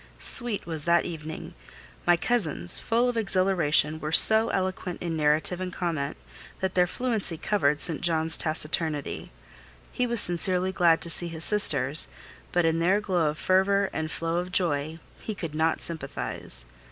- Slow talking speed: No, average, 160 wpm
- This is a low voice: No, medium, 170 Hz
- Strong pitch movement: No, average, 3.1 semitones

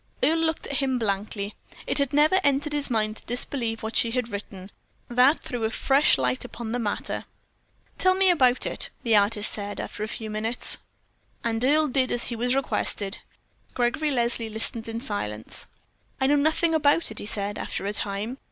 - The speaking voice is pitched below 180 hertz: No, high, 235 Hz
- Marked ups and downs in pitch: No, average, 4.6 semitones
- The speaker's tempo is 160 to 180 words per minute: No, average, 190 wpm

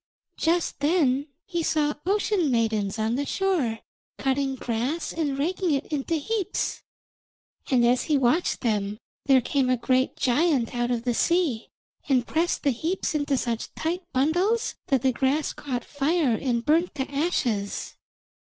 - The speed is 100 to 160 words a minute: Yes, average, 150 wpm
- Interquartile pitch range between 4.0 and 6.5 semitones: Yes, average, 5.1 semitones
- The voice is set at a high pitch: Yes, very high, 275 Hz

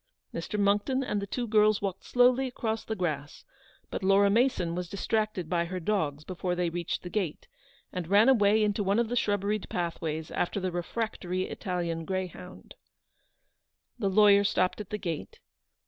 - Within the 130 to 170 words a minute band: Yes, average, 165 wpm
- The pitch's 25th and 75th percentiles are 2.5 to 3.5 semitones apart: Yes, average, 3.2 semitones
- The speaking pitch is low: No, high, 195 Hz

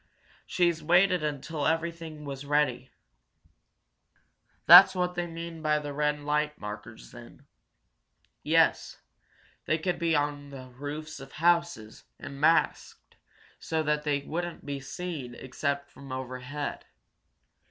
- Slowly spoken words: Yes, slow, 120 wpm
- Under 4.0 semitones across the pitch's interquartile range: Yes, average, 3.0 semitones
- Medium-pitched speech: Yes, medium, 150 Hz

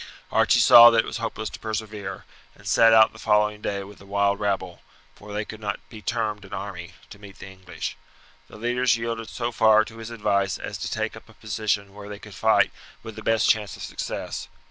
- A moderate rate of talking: No, fast, 220 wpm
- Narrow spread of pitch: Yes, narrow, 1.8 semitones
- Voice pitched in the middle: No, low, 105 Hz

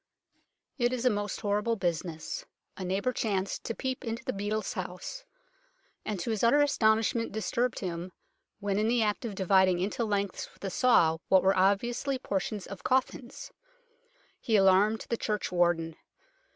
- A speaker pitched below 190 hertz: No, high, 205 Hz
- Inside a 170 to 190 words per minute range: No, average, 155 wpm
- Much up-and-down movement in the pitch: No, average, 3.7 semitones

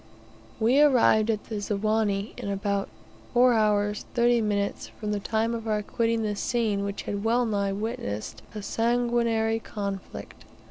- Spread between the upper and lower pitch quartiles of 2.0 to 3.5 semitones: Yes, narrow, 2.4 semitones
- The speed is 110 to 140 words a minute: No, average, 150 wpm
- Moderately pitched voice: No, high, 220 Hz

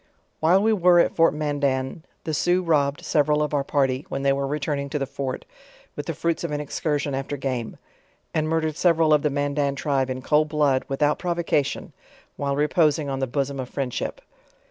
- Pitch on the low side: No, medium, 145 Hz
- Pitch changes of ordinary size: No, narrow, 2.2 semitones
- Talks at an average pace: Yes, average, 190 wpm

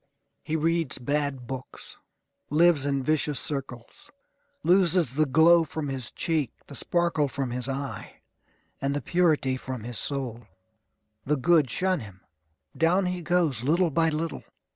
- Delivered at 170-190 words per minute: No, average, 140 wpm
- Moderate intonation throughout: Yes, average, 4.0 semitones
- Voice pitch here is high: No, medium, 145 Hz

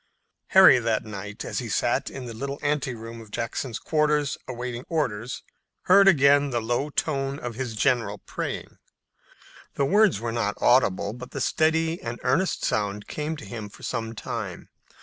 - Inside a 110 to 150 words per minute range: No, average, 165 wpm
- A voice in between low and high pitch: No, low, 125 Hz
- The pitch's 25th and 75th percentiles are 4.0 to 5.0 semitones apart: Yes, average, 4.5 semitones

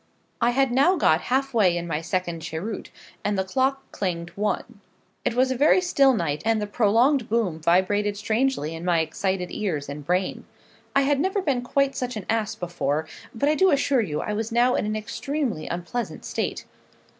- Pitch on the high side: Yes, high, 215 Hz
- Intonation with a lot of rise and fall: Yes, wide, 6.9 semitones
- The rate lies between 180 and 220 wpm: Yes, average, 190 wpm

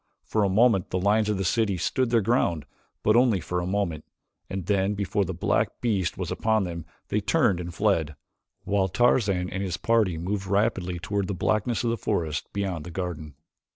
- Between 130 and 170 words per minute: No, average, 195 wpm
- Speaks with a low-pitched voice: Yes, very low, 95 Hz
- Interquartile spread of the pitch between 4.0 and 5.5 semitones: No, average, 3.3 semitones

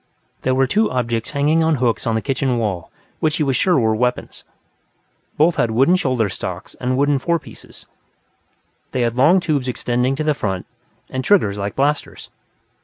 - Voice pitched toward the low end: Yes, low, 130 Hz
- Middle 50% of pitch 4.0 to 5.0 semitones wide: Yes, average, 4.4 semitones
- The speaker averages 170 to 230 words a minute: Yes, average, 180 wpm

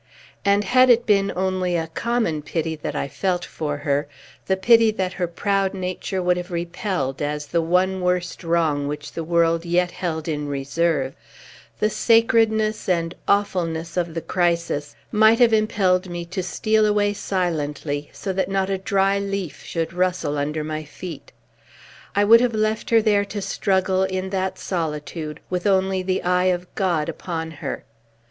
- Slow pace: No, average, 165 wpm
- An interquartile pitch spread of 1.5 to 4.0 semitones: Yes, average, 3.4 semitones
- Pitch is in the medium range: Yes, medium, 180 Hz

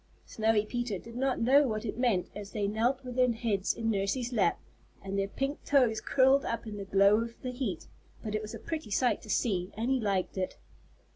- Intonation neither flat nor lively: Yes, average, 3.8 semitones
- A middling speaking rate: No, fast, 220 wpm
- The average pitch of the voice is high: Yes, high, 225 Hz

